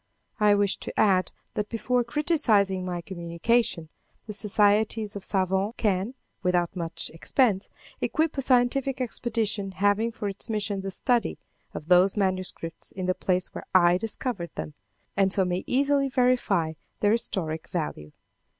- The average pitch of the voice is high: Yes, high, 200 Hz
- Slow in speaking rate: No, average, 145 wpm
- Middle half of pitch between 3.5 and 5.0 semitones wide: Yes, average, 4.0 semitones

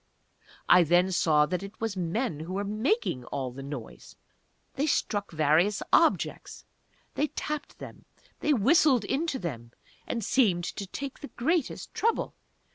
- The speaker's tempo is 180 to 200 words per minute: No, average, 145 wpm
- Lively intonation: Yes, wide, 8.4 semitones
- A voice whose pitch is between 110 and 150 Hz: No, high, 200 Hz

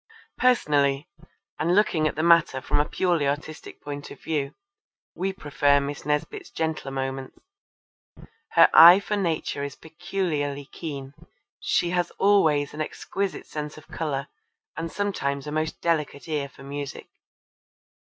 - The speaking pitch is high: No, medium, 150 Hz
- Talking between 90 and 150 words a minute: Yes, average, 140 wpm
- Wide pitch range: No, average, 3.2 semitones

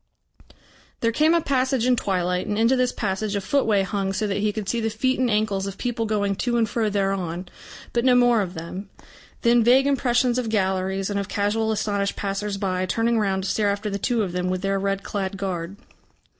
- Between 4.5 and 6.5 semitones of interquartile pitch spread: No, average, 3.3 semitones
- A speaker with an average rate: No, fast, 215 wpm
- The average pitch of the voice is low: No, high, 205 Hz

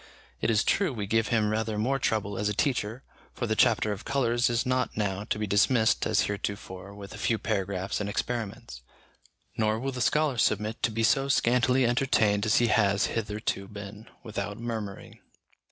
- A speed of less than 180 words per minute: No, average, 185 wpm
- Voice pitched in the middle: No, low, 110 Hz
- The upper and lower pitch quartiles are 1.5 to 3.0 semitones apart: Yes, narrow, 2.6 semitones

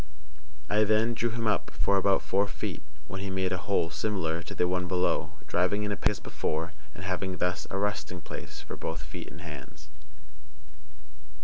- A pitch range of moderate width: Yes, average, 3.0 semitones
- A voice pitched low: Yes, very low, 95 Hz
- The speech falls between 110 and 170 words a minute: No, average, 190 wpm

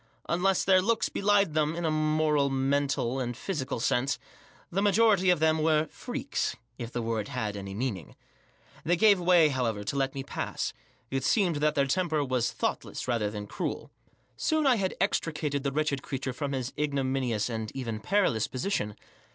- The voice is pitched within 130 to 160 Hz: Yes, medium, 140 Hz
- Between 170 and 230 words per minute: Yes, average, 175 wpm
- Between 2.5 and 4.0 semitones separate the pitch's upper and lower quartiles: No, wide, 5.5 semitones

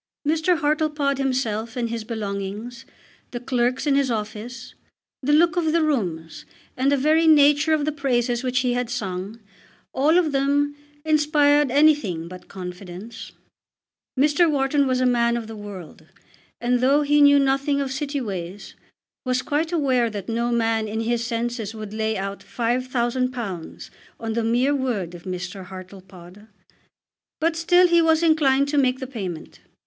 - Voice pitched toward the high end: Yes, very high, 250 Hz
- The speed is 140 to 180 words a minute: Yes, average, 160 wpm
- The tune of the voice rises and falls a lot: No, average, 4.8 semitones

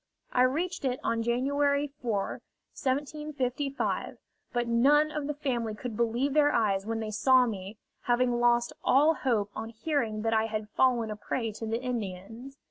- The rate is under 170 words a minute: Yes, average, 160 wpm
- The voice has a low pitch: No, high, 240 Hz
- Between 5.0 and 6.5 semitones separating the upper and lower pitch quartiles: No, average, 3.8 semitones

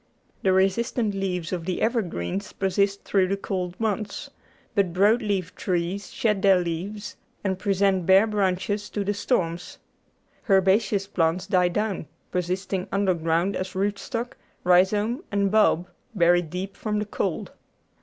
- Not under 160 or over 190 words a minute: No, average, 140 wpm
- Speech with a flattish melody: Yes, narrow, 2.2 semitones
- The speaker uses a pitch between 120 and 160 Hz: No, high, 195 Hz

